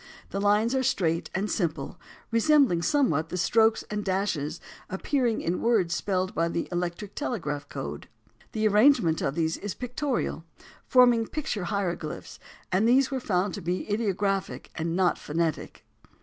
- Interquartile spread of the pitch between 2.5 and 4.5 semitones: No, average, 5.2 semitones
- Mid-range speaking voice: No, high, 195 Hz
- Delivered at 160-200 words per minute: No, average, 150 wpm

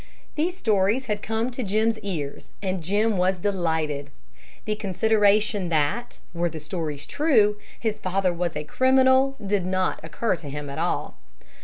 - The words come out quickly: No, average, 155 wpm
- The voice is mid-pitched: No, high, 195 Hz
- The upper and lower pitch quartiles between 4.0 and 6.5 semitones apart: Yes, average, 4.6 semitones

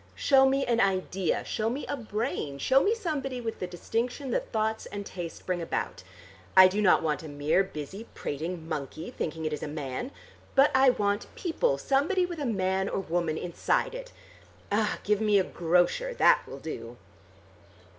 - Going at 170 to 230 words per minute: Yes, average, 180 wpm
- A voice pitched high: Yes, high, 200 Hz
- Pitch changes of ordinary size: No, wide, 8.2 semitones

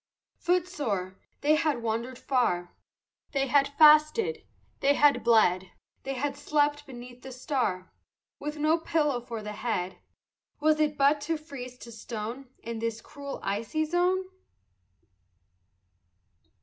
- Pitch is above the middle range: Yes, very high, 275 Hz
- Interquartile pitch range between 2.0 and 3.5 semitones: No, average, 4.6 semitones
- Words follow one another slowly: Yes, slow, 125 wpm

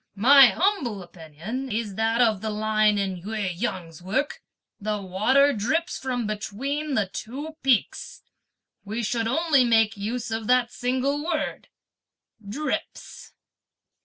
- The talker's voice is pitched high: Yes, high, 225 Hz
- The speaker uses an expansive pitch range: No, average, 4.5 semitones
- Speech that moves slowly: Yes, slow, 130 wpm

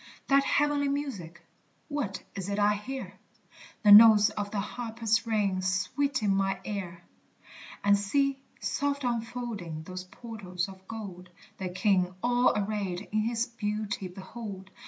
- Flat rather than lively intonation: No, average, 3.8 semitones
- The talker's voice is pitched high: Yes, high, 210 Hz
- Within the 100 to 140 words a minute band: Yes, slow, 135 wpm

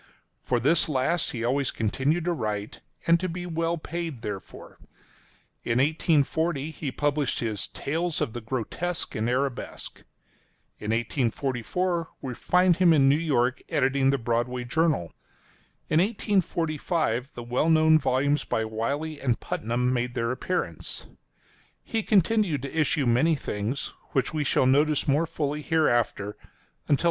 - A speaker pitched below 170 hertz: Yes, medium, 140 Hz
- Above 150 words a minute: No, average, 145 wpm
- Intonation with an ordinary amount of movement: Yes, average, 4.9 semitones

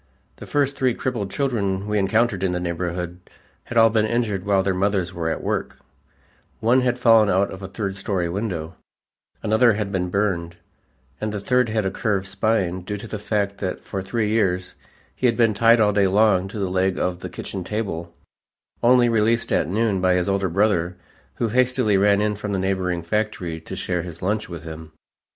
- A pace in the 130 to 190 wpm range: No, average, 200 wpm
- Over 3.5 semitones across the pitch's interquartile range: No, average, 3.2 semitones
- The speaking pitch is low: Yes, low, 100 Hz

